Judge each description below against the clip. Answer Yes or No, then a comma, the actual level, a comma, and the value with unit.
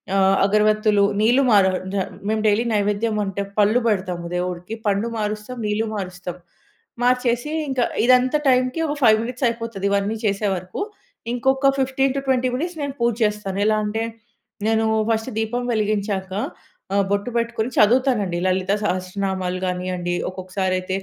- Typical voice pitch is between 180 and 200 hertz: No, high, 215 Hz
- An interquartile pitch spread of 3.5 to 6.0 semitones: Yes, average, 4.0 semitones